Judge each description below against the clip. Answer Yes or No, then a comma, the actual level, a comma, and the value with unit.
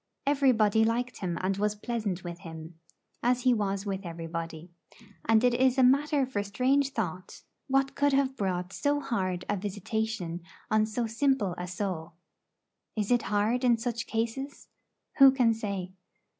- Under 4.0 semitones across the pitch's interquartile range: No, average, 5.2 semitones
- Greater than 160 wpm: No, average, 155 wpm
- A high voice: Yes, high, 220 Hz